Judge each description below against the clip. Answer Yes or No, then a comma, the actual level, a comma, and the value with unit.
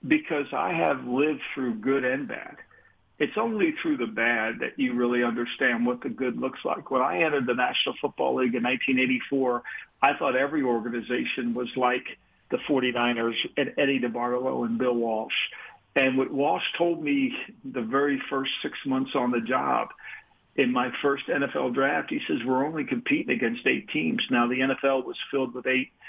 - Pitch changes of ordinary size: No, narrow, 2.3 semitones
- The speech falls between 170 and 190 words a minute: Yes, average, 180 wpm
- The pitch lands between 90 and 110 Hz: No, low, 130 Hz